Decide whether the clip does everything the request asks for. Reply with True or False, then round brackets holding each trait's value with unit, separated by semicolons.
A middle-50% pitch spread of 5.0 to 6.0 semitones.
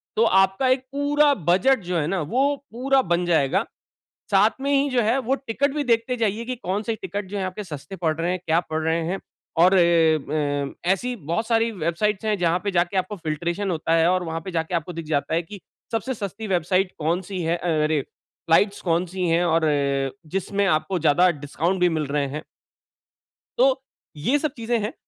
True (5.3 semitones)